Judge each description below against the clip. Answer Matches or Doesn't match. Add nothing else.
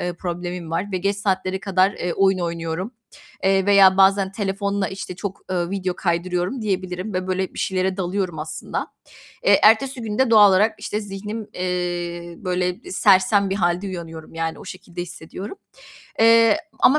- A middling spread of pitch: Doesn't match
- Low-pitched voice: Doesn't match